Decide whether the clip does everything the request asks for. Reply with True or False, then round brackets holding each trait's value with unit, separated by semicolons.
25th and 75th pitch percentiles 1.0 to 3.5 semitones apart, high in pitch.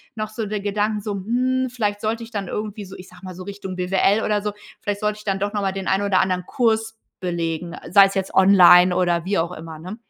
True (2.5 semitones; 200 Hz)